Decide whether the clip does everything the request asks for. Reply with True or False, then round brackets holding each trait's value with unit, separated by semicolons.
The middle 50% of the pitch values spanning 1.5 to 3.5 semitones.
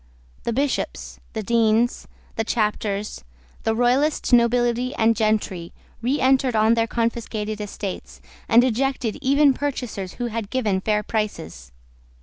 True (2.7 semitones)